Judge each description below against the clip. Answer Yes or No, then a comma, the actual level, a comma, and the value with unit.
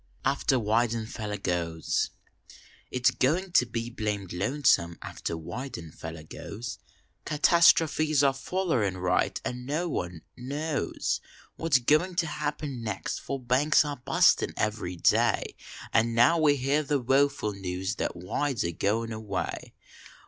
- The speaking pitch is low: Yes, low, 120 Hz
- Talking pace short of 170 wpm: Yes, slow, 135 wpm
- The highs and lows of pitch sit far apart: Yes, wide, 6.5 semitones